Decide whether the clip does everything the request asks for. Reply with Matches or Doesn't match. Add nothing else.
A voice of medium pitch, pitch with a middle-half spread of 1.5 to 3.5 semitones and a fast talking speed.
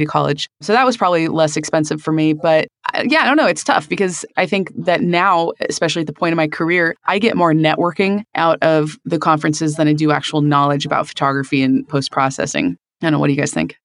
Matches